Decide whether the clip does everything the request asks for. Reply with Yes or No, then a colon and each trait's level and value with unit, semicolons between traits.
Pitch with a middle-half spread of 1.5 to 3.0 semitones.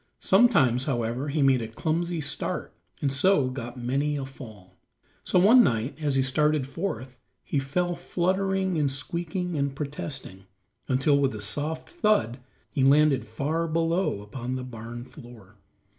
No: average, 4.8 semitones